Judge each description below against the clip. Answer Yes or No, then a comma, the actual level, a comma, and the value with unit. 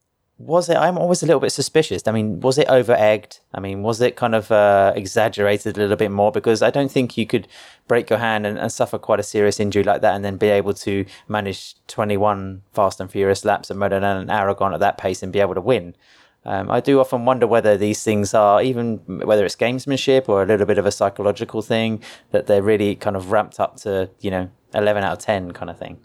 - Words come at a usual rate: No, fast, 245 wpm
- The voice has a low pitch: Yes, low, 105 Hz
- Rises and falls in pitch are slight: Yes, narrow, 2.3 semitones